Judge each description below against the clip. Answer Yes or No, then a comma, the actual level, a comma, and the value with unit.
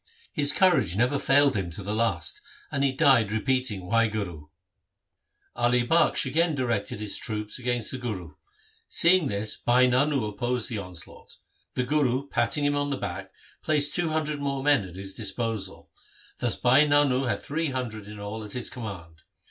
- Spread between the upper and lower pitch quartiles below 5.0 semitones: No, average, 5.3 semitones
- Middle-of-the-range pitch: No, low, 120 Hz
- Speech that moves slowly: No, average, 175 wpm